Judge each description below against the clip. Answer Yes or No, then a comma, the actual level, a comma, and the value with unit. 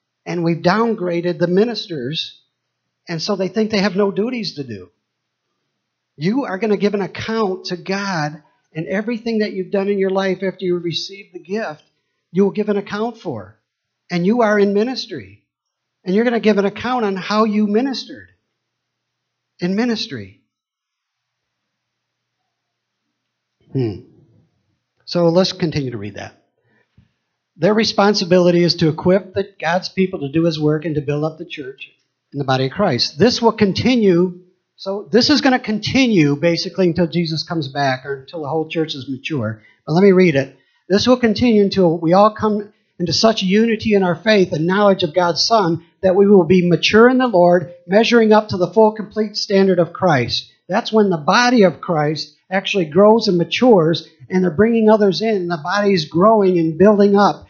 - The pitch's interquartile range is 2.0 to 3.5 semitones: No, average, 4.5 semitones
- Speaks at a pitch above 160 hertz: Yes, medium, 185 Hz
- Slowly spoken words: No, average, 180 wpm